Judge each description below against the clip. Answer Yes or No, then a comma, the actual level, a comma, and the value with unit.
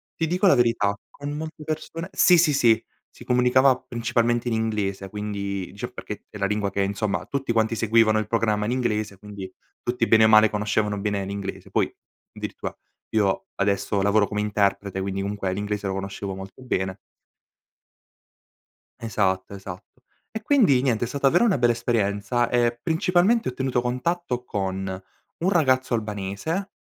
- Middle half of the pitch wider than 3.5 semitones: Yes, average, 4.1 semitones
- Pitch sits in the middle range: No, low, 110 Hz